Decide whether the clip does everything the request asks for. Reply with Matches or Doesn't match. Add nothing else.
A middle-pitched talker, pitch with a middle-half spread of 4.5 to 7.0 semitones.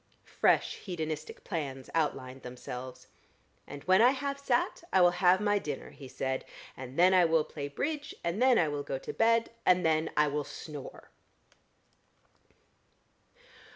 Matches